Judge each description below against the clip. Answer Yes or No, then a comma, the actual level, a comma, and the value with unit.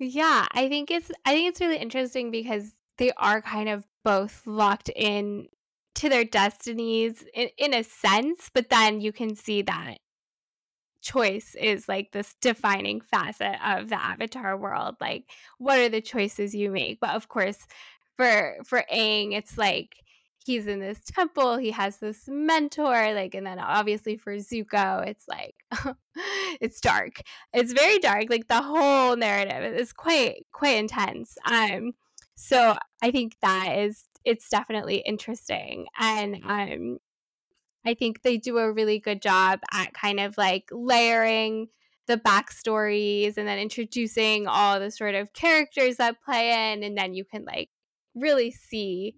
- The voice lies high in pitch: Yes, high, 220 Hz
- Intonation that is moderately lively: Yes, average, 3.5 semitones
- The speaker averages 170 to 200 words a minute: No, average, 155 wpm